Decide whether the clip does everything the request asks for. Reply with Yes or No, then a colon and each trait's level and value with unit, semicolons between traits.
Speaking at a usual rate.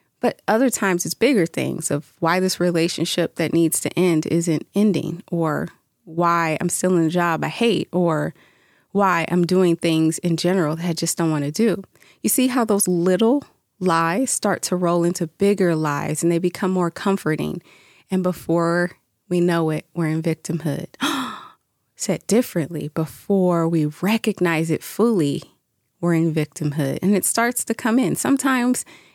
Yes: average, 165 wpm